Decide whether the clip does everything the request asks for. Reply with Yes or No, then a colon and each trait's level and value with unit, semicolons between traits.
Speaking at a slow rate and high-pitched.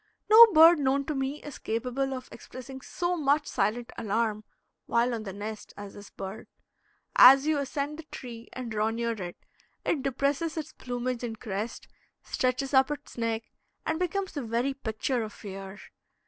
No: average, 170 wpm; very high, 255 Hz